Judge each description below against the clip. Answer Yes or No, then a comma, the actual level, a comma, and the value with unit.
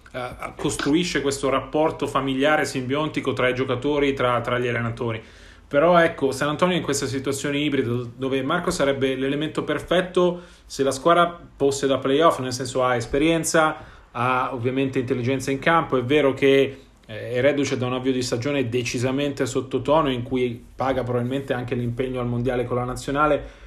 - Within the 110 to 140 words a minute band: No, average, 165 wpm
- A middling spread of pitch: No, narrow, 2.2 semitones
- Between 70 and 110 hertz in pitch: No, low, 135 Hz